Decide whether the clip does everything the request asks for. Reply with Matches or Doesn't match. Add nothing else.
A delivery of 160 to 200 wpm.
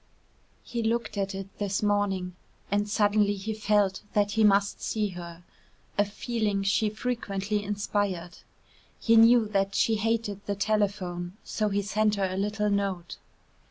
Doesn't match